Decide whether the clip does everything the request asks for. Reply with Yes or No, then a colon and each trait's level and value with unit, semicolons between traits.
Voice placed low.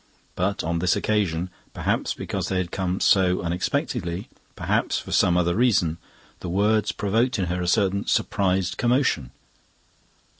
Yes: very low, 95 Hz